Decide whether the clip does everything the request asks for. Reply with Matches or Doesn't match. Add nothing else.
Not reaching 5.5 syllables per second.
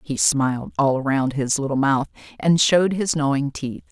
Matches